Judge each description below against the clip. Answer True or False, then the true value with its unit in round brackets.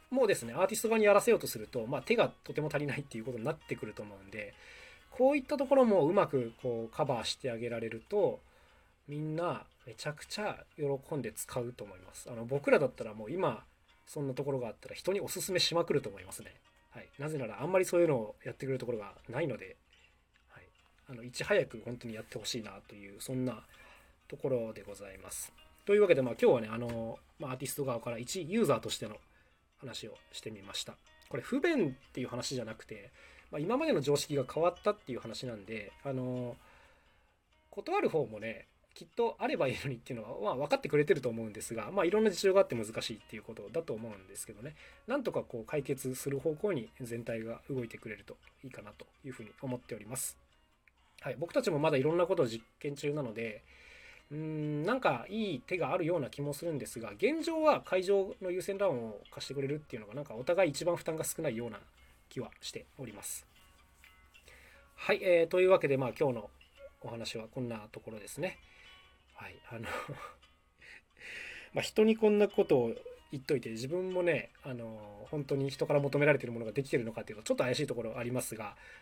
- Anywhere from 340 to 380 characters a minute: False (430 characters per minute)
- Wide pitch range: True (7.4 semitones)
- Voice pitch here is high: False (135 Hz)